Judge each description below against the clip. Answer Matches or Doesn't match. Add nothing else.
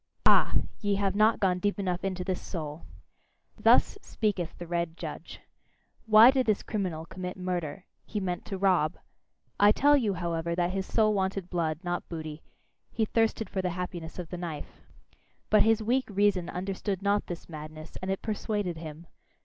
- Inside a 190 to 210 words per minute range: Doesn't match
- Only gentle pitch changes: Doesn't match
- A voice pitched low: Doesn't match